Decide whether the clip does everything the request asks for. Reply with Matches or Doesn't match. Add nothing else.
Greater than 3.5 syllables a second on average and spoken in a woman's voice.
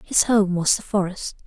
Matches